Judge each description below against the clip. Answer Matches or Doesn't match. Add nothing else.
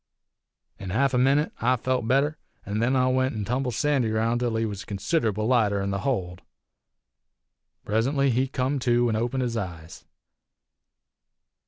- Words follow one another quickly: Doesn't match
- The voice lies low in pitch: Matches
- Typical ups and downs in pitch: Matches